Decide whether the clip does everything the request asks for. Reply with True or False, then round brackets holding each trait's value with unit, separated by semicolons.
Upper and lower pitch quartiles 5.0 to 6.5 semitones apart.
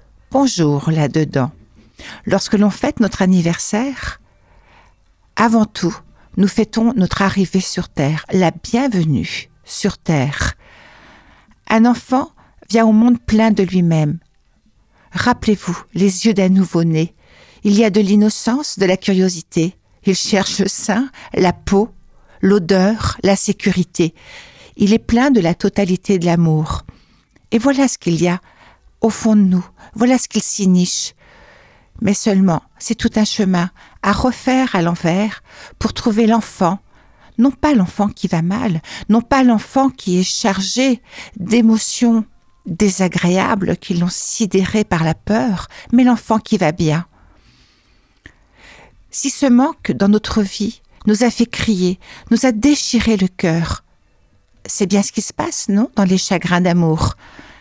False (4.1 semitones)